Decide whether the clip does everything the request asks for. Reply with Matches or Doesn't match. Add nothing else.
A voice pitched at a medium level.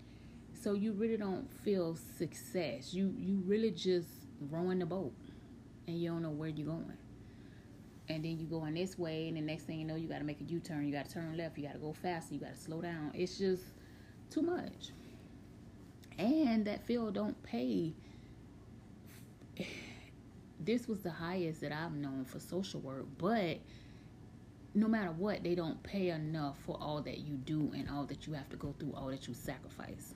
Matches